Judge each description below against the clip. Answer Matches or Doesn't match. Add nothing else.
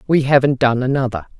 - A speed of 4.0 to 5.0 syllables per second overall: Doesn't match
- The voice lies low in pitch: Matches